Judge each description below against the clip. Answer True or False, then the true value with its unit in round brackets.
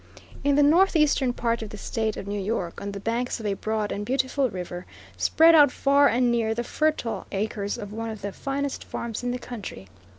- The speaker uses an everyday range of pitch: True (4.8 semitones)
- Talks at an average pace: False (210 wpm)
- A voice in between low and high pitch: False (230 Hz)